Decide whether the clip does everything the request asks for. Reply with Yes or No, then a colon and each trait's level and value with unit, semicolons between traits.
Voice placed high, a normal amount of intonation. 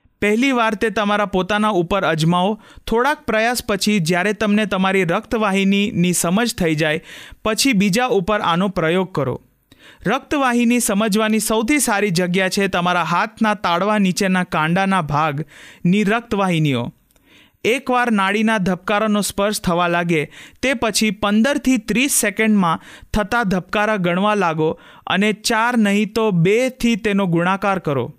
Yes: high, 205 Hz; average, 3.6 semitones